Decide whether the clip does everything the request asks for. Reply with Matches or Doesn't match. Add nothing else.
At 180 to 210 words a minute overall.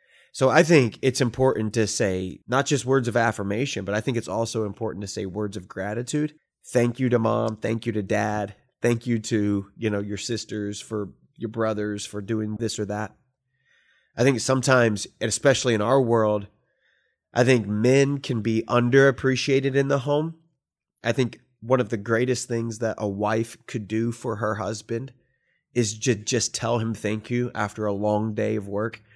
Matches